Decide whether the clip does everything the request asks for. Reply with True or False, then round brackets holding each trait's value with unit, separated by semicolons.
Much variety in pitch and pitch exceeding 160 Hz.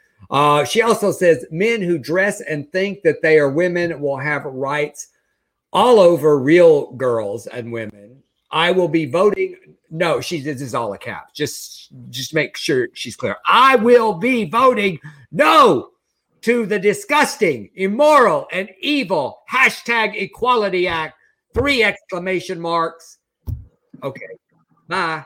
True (7.2 semitones; 185 Hz)